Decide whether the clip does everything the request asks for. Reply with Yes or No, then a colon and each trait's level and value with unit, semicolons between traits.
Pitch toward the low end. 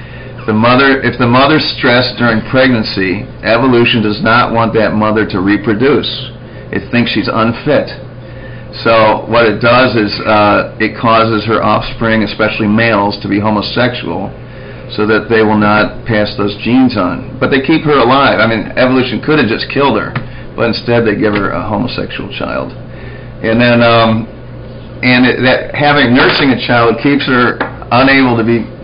Yes: low, 120 Hz